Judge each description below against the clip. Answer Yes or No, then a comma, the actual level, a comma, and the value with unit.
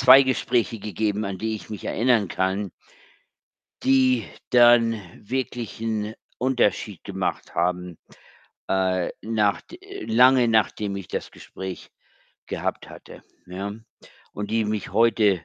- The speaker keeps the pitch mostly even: No, average, 3.3 semitones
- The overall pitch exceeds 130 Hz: No, low, 110 Hz